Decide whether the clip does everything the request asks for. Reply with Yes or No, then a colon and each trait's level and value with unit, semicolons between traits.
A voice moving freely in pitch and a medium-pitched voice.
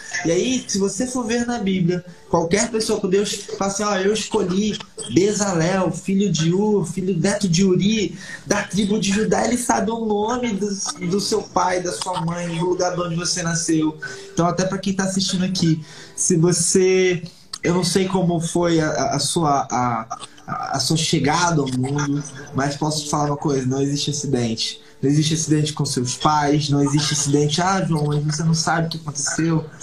No: average, 4.3 semitones; medium, 175 Hz